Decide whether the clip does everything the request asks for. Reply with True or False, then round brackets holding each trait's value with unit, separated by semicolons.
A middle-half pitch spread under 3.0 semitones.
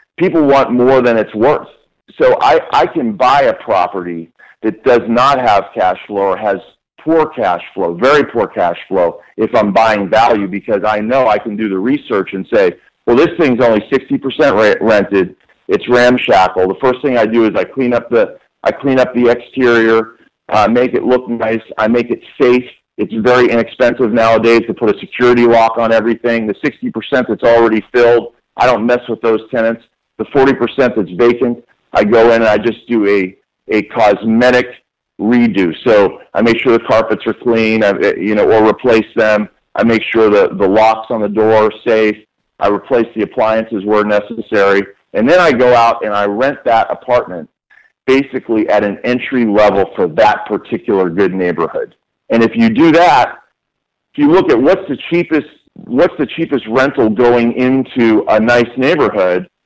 True (2.4 semitones)